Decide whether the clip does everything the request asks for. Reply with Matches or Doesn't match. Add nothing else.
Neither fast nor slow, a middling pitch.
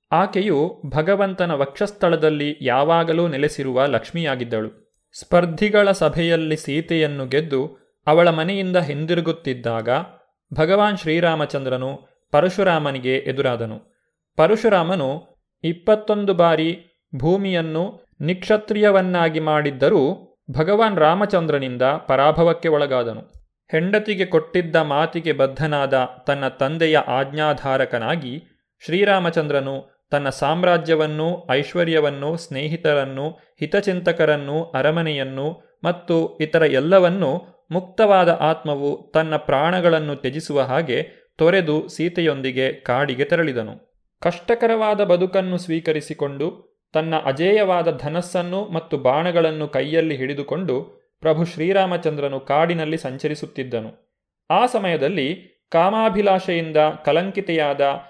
Matches